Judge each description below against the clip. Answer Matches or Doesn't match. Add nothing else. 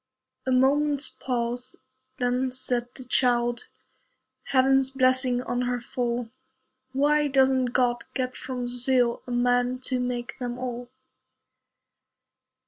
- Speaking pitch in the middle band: Doesn't match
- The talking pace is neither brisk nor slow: Doesn't match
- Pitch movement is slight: Matches